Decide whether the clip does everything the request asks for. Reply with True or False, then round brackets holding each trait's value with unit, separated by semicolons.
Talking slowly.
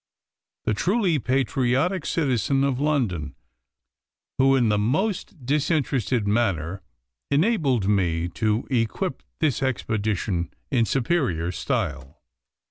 True (100 wpm)